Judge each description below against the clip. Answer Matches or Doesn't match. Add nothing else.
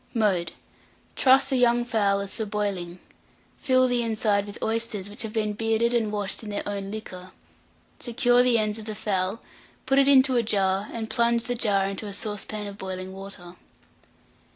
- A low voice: Doesn't match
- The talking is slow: Doesn't match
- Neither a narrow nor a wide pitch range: Matches